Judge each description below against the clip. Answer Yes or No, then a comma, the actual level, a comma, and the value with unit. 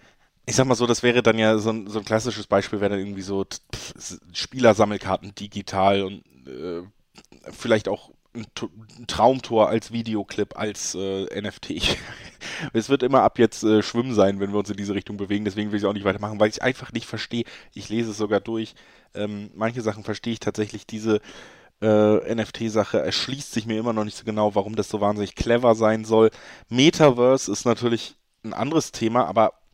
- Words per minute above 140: Yes, fast, 190 wpm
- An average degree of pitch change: No, narrow, 2.1 semitones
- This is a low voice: Yes, low, 110 Hz